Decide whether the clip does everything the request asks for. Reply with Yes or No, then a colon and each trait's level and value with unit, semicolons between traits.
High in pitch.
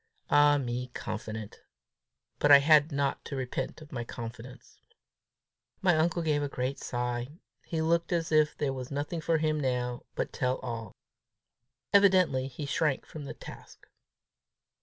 No: medium, 140 Hz